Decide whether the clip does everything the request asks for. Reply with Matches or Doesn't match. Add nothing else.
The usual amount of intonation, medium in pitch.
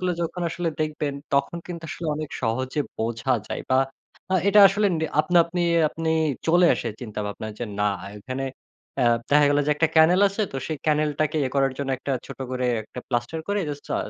Matches